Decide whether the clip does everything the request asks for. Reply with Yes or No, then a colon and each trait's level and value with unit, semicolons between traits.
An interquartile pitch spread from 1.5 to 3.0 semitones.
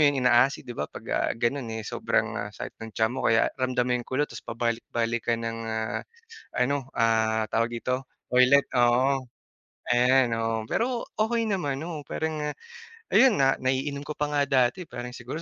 No: average, 3.4 semitones